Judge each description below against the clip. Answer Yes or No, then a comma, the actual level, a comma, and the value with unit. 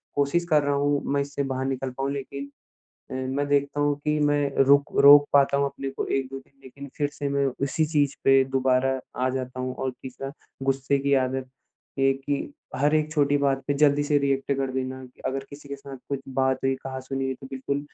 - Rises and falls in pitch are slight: Yes, narrow, 1.2 semitones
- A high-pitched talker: No, medium, 140 Hz